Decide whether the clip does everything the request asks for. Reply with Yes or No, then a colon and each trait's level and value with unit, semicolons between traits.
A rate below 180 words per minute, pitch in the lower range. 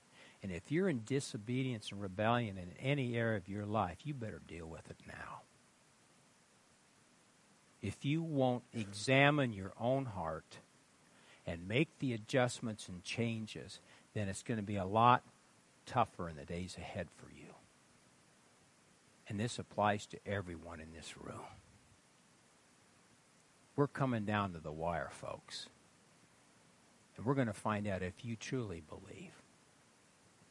Yes: average, 140 wpm; low, 110 Hz